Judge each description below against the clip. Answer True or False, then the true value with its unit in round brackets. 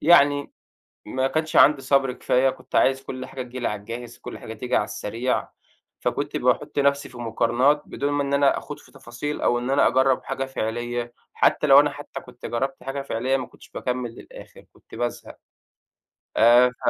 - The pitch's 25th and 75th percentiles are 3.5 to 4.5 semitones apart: False (2.5 semitones)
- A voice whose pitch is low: True (130 Hz)